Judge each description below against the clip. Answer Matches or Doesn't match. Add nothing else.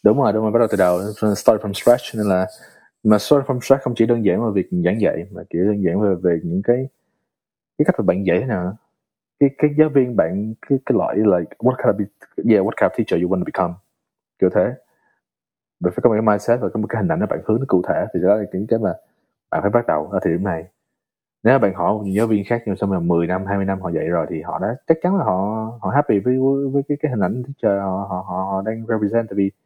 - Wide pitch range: Doesn't match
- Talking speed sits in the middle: Doesn't match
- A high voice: Doesn't match